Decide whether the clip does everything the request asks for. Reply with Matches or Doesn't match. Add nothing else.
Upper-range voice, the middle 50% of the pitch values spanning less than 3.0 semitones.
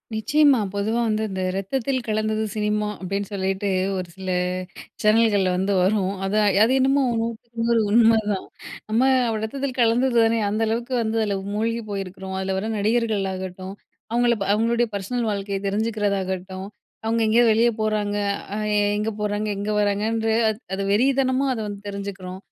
Matches